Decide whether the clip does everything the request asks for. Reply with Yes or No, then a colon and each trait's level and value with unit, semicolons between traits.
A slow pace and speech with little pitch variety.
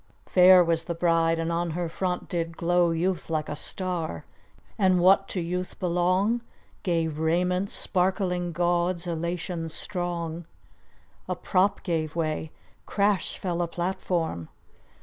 Yes: slow, 130 wpm; narrow, 1.8 semitones